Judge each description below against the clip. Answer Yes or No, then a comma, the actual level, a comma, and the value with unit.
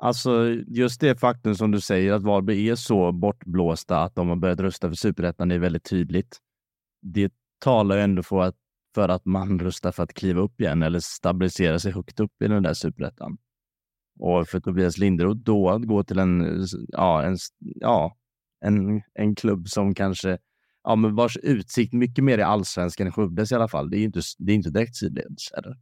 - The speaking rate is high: Yes, fast, 200 wpm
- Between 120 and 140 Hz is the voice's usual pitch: No, low, 100 Hz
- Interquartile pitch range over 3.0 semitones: Yes, average, 3.4 semitones